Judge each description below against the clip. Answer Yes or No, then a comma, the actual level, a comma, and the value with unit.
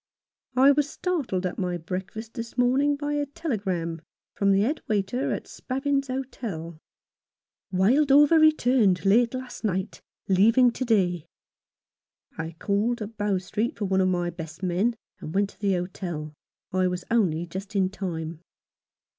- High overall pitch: Yes, high, 200 Hz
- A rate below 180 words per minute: Yes, average, 155 wpm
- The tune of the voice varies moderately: No, wide, 5.9 semitones